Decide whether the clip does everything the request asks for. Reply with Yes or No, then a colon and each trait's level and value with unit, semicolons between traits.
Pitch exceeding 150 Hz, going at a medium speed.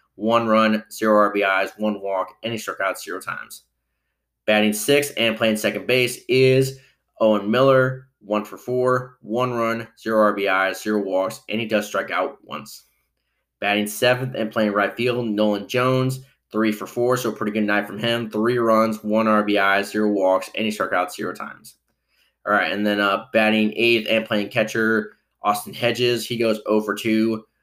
No: low, 110 Hz; average, 180 wpm